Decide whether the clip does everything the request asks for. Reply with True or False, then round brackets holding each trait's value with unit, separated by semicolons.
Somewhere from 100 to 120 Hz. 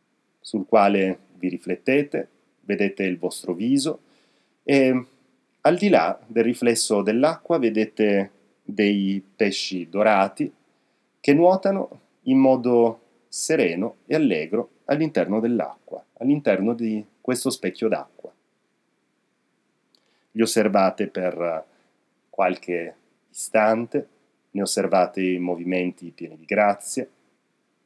True (110 Hz)